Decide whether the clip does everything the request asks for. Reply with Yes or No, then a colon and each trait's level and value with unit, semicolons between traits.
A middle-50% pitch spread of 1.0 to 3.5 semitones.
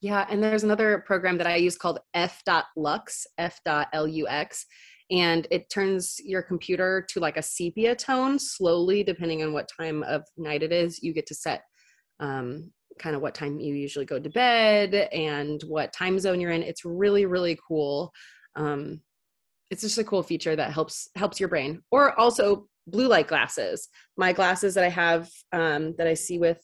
No: average, 4.3 semitones